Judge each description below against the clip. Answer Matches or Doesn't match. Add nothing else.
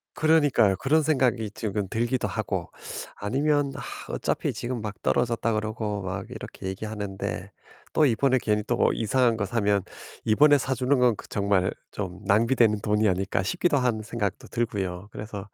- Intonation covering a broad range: Doesn't match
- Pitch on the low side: Matches